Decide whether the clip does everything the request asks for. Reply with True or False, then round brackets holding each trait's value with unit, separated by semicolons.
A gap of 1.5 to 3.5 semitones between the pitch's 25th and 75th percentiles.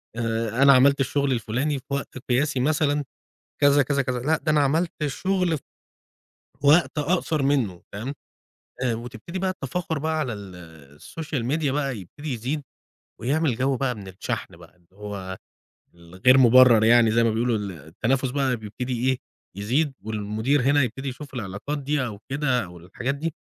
False (4.6 semitones)